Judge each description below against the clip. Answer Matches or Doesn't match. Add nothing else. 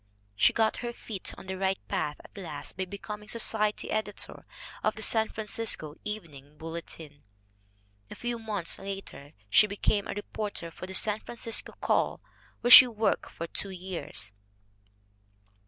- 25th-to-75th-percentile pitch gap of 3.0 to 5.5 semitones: Matches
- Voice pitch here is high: Matches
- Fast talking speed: Doesn't match